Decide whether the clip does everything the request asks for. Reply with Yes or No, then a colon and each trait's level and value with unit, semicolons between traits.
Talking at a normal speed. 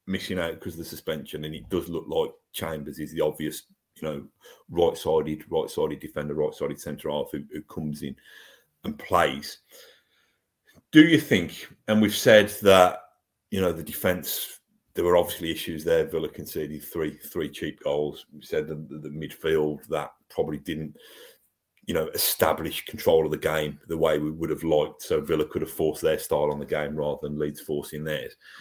Yes: average, 180 wpm